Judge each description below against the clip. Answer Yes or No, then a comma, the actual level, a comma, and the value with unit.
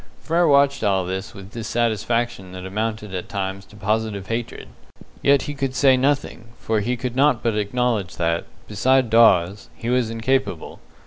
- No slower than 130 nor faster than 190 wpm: Yes, average, 165 wpm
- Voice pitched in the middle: No, low, 115 Hz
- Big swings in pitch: No, average, 4.4 semitones